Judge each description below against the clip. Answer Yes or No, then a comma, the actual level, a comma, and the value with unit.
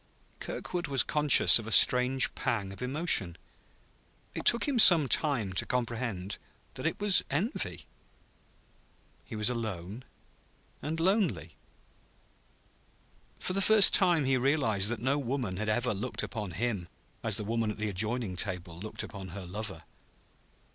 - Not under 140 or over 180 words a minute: Yes, average, 145 wpm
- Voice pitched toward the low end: Yes, low, 120 Hz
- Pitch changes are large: Yes, wide, 6.0 semitones